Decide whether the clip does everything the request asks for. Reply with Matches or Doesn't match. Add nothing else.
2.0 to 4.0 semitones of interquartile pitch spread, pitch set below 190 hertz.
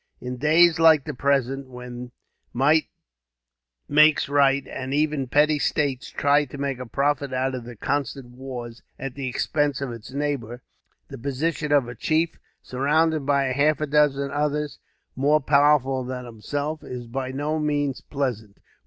Matches